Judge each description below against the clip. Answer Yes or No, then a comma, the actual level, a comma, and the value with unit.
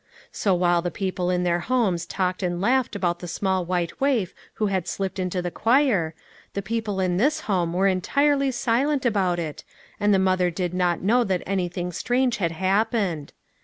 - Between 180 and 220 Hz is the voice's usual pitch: Yes, high, 190 Hz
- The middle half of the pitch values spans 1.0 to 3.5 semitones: No, average, 4.0 semitones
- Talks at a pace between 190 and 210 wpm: Yes, average, 195 wpm